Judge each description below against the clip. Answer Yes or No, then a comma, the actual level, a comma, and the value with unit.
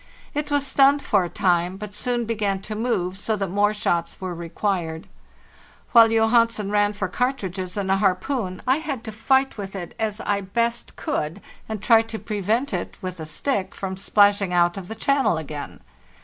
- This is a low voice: No, high, 205 Hz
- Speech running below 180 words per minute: No, average, 185 wpm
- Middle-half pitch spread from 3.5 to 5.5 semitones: Yes, average, 3.8 semitones